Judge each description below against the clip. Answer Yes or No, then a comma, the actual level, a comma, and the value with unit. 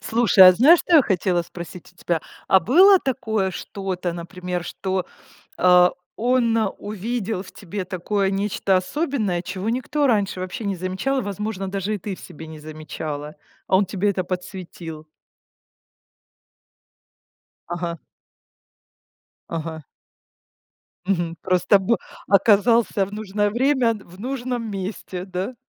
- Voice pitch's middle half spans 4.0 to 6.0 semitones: No, average, 3.6 semitones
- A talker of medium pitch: No, high, 195 Hz